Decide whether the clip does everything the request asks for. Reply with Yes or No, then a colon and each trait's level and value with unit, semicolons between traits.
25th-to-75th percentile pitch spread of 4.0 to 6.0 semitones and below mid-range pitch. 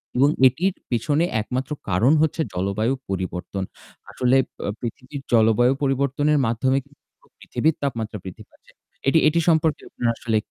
Yes: average, 4.4 semitones; low, 130 Hz